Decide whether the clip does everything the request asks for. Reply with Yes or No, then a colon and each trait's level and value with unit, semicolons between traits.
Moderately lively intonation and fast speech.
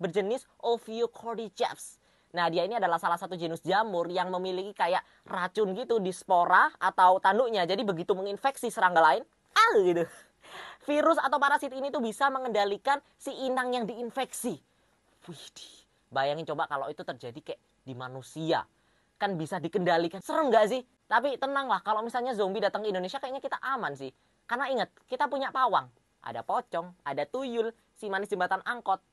No: wide, 5.9 semitones; fast, 160 wpm